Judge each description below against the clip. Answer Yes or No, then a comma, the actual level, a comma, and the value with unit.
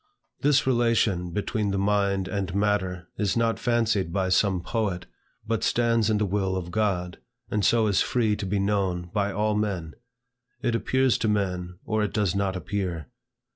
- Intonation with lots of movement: No, average, 2.7 semitones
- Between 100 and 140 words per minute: No, average, 175 wpm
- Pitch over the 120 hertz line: No, low, 100 Hz